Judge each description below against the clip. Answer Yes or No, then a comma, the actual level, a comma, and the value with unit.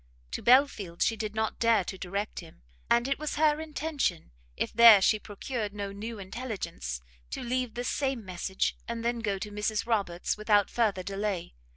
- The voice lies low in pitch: No, high, 215 Hz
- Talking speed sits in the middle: Yes, average, 180 wpm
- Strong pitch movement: No, average, 3.3 semitones